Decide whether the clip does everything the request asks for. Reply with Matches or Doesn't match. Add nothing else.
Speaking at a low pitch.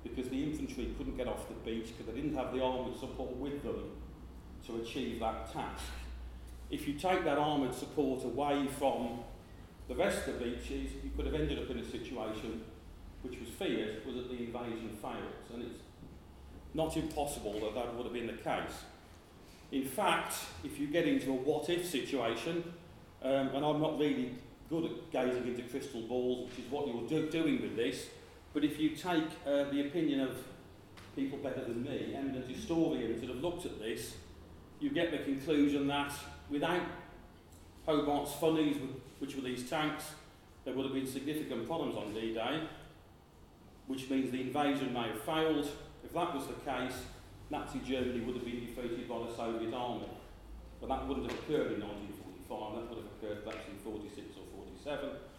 Matches